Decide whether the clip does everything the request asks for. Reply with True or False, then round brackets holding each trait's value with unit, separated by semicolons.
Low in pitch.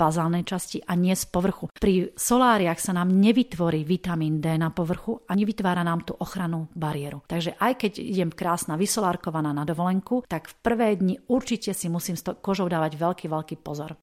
False (180 Hz)